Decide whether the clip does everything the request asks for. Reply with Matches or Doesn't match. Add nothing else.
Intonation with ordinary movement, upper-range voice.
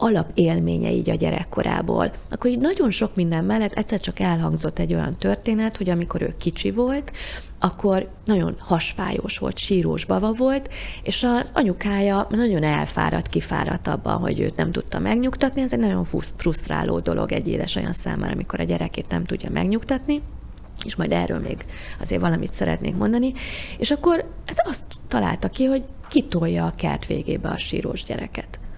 Doesn't match